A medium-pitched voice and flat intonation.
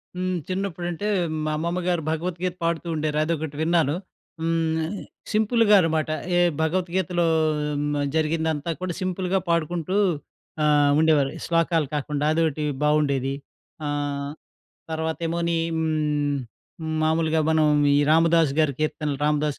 Yes: medium, 160 Hz; narrow, 2.2 semitones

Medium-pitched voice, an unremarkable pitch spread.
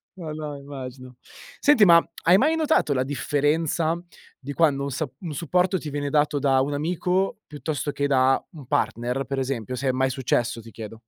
Yes: medium, 145 Hz; average, 3.7 semitones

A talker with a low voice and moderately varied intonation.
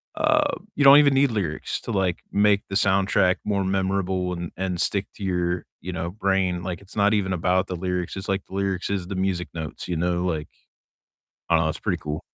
No: very low, 95 Hz; narrow, 2.0 semitones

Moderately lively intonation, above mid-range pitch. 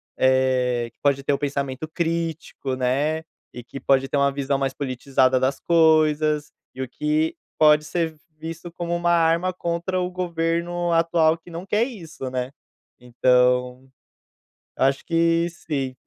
No: average, 4.2 semitones; medium, 155 Hz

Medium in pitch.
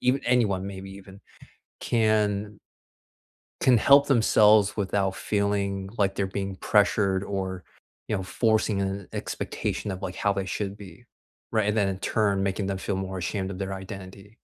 No: low, 100 Hz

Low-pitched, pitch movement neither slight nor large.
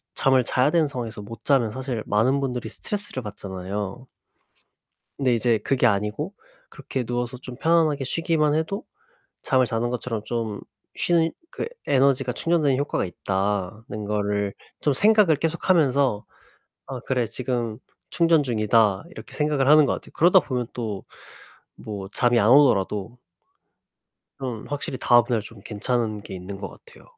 Yes: low, 125 Hz; average, 5.0 semitones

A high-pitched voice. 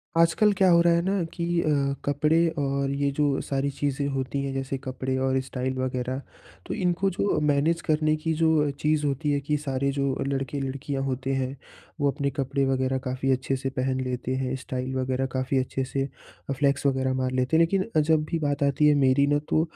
No: medium, 140 Hz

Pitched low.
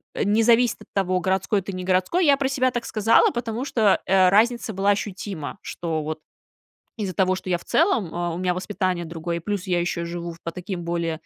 No: medium, 185 Hz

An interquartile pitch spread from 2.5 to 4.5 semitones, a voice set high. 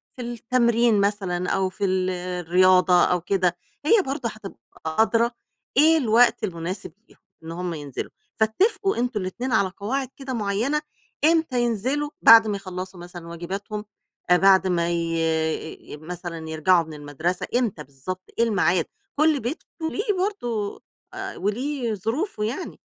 No: wide, 5.5 semitones; high, 200 Hz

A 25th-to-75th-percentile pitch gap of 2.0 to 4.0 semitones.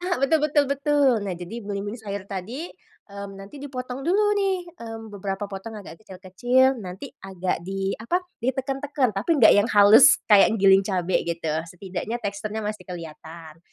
No: average, 5.3 semitones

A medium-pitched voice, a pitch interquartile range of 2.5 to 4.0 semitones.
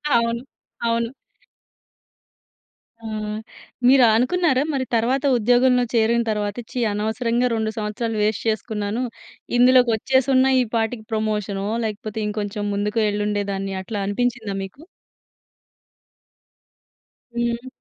No: high, 225 Hz; average, 2.9 semitones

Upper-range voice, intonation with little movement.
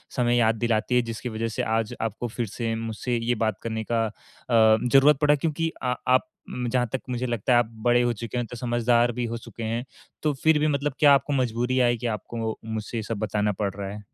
No: low, 120 Hz; narrow, 2.0 semitones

